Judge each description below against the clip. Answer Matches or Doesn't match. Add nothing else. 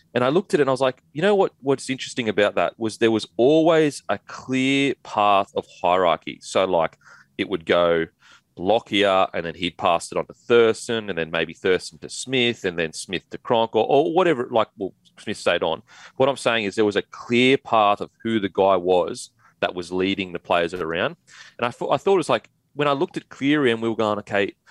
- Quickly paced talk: Matches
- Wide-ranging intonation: Matches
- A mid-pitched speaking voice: Doesn't match